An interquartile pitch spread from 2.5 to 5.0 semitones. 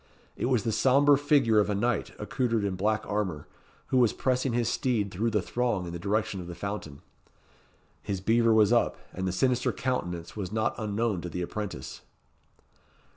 Yes: average, 3.8 semitones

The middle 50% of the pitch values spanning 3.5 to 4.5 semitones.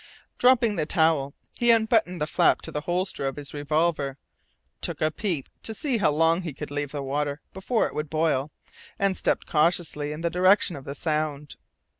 Yes: average, 4.1 semitones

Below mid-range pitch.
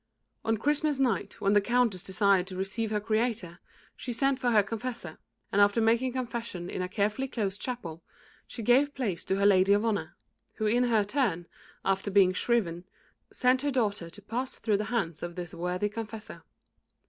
No: high, 210 Hz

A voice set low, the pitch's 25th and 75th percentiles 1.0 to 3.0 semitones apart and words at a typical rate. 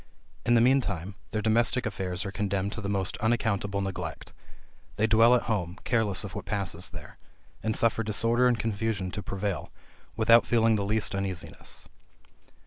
Yes: low, 105 Hz; average, 2.7 semitones; average, 165 wpm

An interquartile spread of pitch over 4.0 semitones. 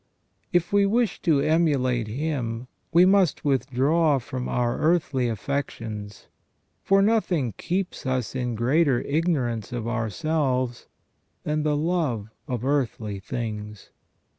Yes: wide, 5.4 semitones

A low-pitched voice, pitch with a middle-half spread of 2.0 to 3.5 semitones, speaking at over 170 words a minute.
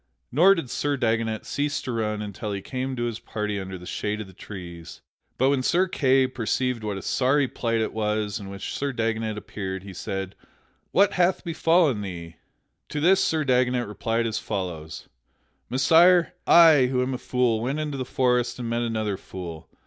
No: low, 115 Hz; average, 4.4 semitones; average, 185 wpm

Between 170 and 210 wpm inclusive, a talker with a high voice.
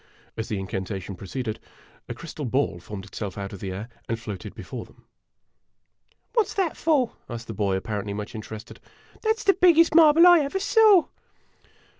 No: average, 185 wpm; low, 115 Hz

